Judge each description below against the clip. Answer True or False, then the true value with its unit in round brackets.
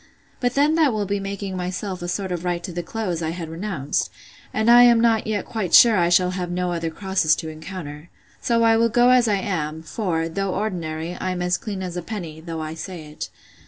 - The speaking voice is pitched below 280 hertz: True (185 Hz)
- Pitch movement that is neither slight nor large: True (4.4 semitones)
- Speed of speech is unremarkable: False (235 wpm)